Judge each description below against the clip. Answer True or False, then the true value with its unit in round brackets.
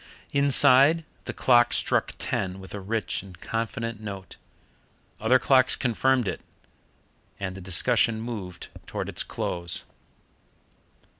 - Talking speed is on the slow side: True (120 wpm)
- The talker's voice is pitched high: False (115 Hz)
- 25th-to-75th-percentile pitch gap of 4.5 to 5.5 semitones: True (5.0 semitones)